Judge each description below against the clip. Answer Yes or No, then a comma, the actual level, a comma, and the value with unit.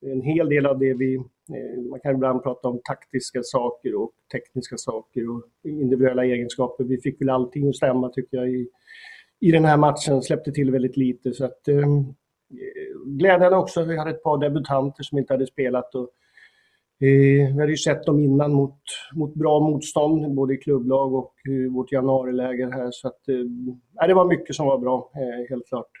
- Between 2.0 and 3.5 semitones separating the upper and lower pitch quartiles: Yes, average, 2.8 semitones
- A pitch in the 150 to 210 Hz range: No, low, 135 Hz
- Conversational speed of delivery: Yes, average, 185 wpm